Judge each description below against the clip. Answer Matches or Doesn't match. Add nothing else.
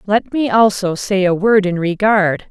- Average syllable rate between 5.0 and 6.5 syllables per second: Doesn't match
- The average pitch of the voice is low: Doesn't match